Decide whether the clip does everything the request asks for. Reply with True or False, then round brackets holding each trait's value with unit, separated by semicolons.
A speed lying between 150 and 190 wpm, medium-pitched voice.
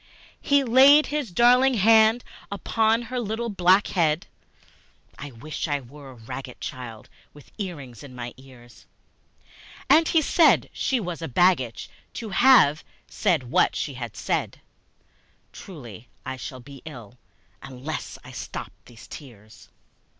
False (135 wpm; 155 Hz)